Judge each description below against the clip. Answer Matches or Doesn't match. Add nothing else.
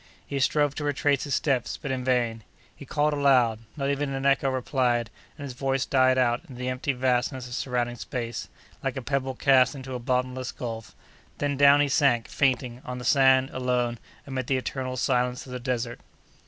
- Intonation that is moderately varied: Doesn't match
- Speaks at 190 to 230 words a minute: Matches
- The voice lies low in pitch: Matches